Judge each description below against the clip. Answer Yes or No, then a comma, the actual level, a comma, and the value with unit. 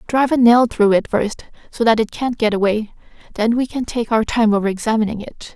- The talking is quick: Yes, fast, 225 wpm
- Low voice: No, high, 225 Hz